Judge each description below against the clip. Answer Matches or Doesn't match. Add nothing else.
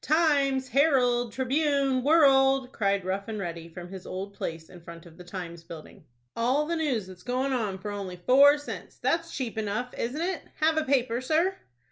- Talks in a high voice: Matches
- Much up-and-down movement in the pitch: Matches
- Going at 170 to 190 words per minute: Matches